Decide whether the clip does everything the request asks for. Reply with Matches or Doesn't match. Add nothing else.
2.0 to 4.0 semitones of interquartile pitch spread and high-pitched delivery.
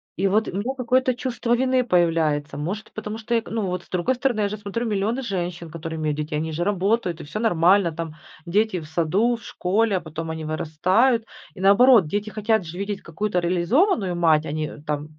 Doesn't match